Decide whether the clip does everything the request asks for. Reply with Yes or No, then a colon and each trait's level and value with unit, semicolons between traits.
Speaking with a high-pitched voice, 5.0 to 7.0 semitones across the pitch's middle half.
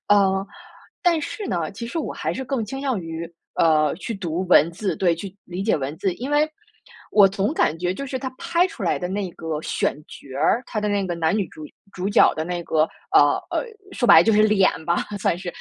Yes: high, 195 Hz; average, 5.3 semitones